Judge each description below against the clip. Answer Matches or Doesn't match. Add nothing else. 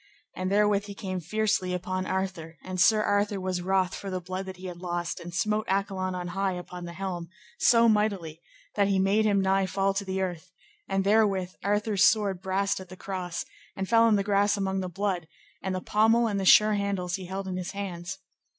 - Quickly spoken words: Matches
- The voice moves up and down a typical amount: Doesn't match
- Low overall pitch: Doesn't match